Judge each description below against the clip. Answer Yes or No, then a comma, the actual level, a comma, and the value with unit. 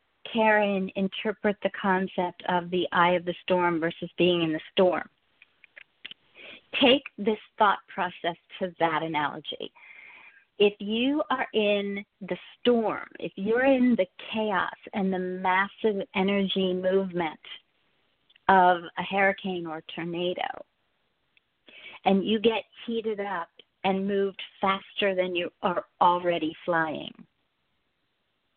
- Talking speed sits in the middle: No, slow, 120 wpm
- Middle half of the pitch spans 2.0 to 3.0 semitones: Yes, narrow, 2.6 semitones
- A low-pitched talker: No, high, 190 Hz